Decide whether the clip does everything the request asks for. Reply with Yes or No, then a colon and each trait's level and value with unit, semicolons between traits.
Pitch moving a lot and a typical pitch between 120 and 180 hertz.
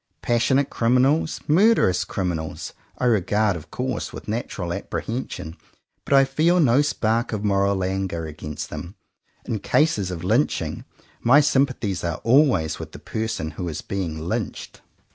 No: wide, 6.7 semitones; low, 105 Hz